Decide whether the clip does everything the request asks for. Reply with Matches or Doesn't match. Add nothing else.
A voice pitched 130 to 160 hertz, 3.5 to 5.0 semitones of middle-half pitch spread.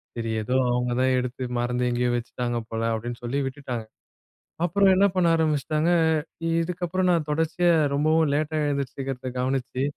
Matches